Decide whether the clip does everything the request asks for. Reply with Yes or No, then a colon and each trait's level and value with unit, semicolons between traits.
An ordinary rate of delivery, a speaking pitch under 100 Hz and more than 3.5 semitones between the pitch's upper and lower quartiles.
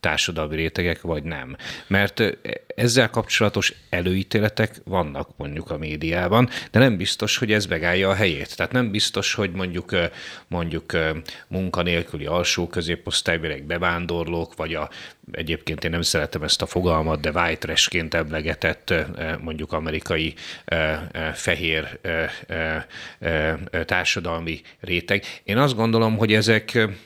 Yes: average, 120 wpm; very low, 85 Hz; average, 3.9 semitones